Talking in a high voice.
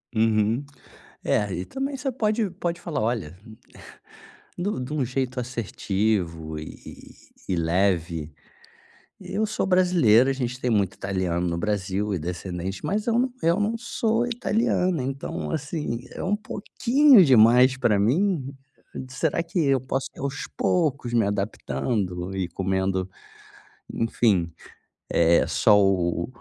No: low, 120 Hz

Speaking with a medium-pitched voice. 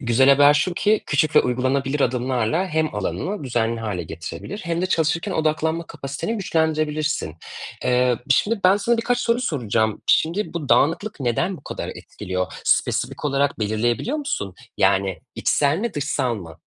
Yes: medium, 145 Hz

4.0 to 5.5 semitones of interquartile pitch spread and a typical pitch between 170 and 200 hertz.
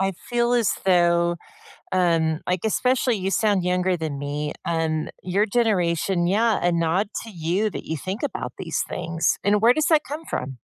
Yes: average, 4.5 semitones; medium, 185 Hz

